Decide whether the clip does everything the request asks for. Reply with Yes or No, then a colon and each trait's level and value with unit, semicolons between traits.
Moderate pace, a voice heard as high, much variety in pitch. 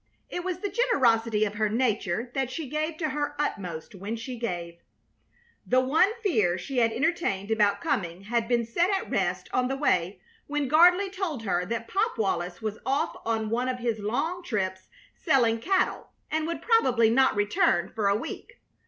Yes: average, 180 wpm; high, 235 Hz; wide, 6.7 semitones